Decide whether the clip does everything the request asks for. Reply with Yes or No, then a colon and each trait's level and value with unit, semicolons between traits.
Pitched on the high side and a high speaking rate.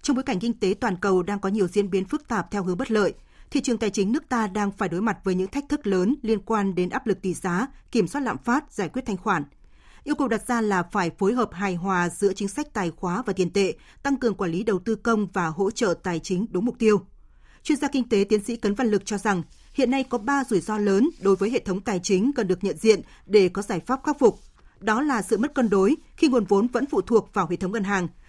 Yes: high, 205 Hz; fast, 280 wpm